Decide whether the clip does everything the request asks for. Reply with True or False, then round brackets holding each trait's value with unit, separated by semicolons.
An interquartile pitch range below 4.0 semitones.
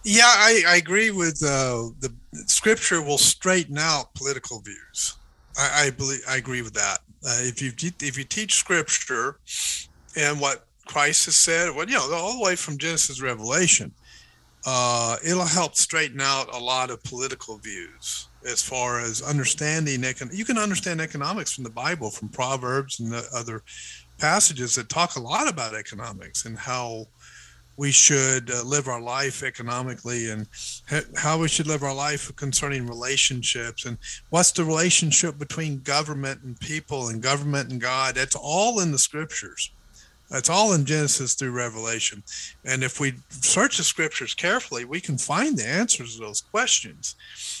False (4.6 semitones)